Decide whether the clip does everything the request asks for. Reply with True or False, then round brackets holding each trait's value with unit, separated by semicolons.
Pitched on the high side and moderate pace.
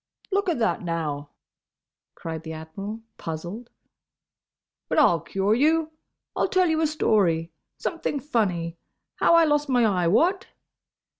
False (215 Hz; 130 wpm)